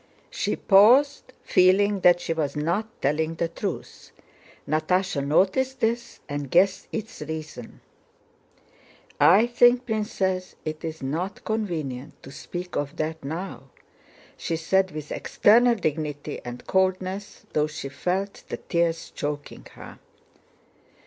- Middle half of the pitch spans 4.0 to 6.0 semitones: Yes, average, 4.7 semitones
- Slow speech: Yes, slow, 120 wpm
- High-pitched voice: No, medium, 175 Hz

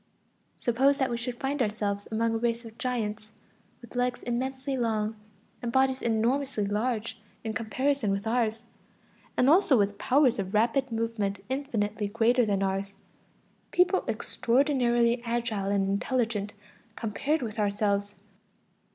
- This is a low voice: No, high, 230 Hz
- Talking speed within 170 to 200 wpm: No, slow, 135 wpm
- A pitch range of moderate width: Yes, average, 3.3 semitones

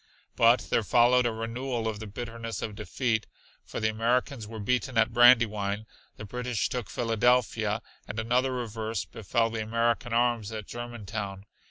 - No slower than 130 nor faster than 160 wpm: Yes, average, 155 wpm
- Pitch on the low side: Yes, low, 115 Hz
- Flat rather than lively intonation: Yes, narrow, 1.9 semitones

